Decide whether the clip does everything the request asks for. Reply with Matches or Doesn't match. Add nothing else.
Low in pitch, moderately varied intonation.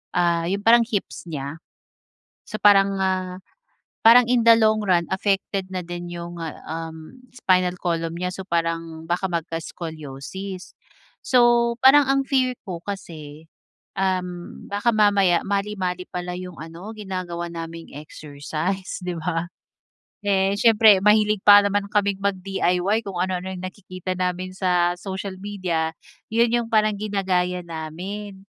Doesn't match